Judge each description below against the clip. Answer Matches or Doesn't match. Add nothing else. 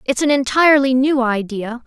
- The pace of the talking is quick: Doesn't match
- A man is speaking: Doesn't match